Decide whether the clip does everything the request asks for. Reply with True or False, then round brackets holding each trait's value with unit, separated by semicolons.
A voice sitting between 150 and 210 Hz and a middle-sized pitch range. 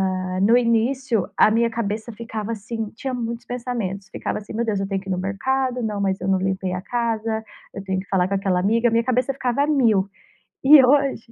False (225 Hz; 3.8 semitones)